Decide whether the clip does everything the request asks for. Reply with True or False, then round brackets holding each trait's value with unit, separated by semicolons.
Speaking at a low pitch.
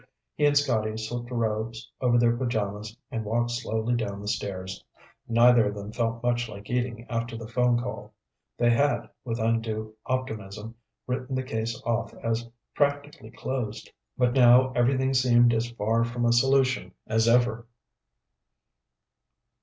True (115 Hz)